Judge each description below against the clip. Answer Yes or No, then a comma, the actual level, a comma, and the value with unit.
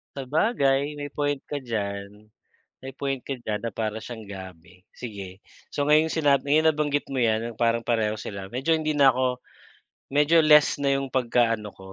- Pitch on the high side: No, low, 130 Hz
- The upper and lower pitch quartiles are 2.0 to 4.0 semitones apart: No, average, 4.8 semitones